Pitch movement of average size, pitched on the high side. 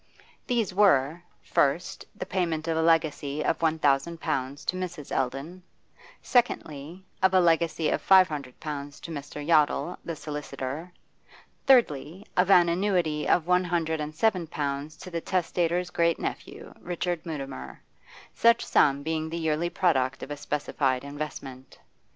No: average, 3.5 semitones; medium, 160 Hz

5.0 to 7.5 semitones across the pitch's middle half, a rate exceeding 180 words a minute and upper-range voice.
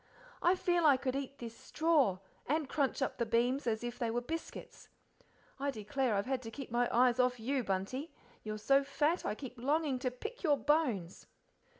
No: average, 3.7 semitones; average, 195 wpm; very high, 260 Hz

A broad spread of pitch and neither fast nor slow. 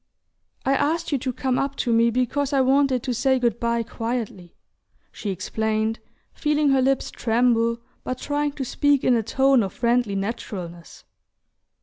No: average, 3.1 semitones; average, 160 wpm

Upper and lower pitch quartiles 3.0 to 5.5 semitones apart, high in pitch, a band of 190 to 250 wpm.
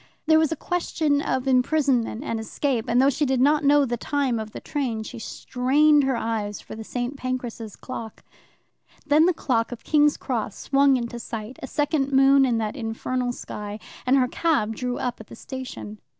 Yes: average, 3.8 semitones; very high, 255 Hz; average, 195 wpm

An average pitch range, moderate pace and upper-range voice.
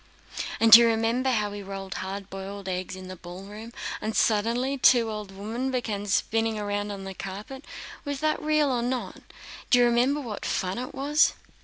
Yes: average, 4.0 semitones; average, 185 wpm; high, 220 Hz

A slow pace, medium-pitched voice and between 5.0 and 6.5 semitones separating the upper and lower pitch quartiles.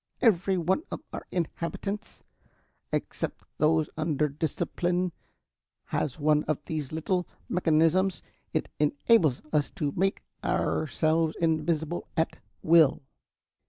No: slow, 105 wpm; medium, 160 Hz; average, 2.8 semitones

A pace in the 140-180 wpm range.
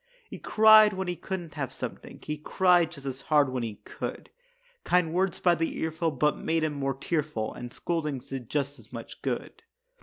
No: average, 190 wpm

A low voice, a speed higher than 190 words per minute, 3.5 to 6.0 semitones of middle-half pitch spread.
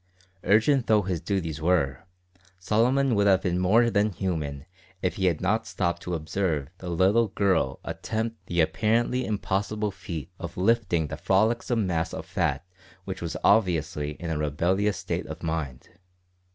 No: very low, 95 Hz; average, 155 wpm; average, 4.6 semitones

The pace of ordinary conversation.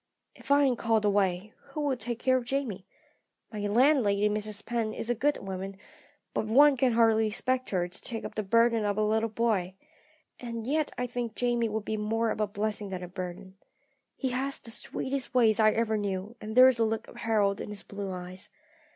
No: fast, 210 wpm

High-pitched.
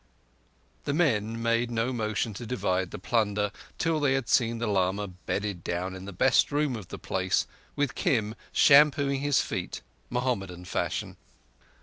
No: low, 115 Hz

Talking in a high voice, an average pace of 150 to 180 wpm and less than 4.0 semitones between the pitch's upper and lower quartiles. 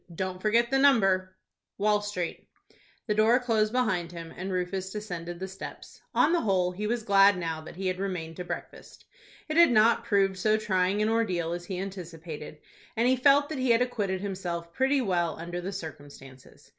No: high, 195 Hz; average, 195 wpm; average, 3.6 semitones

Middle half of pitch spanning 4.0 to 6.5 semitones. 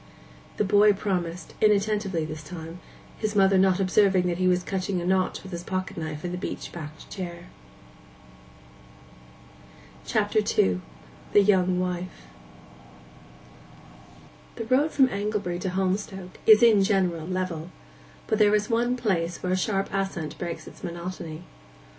No: average, 2.9 semitones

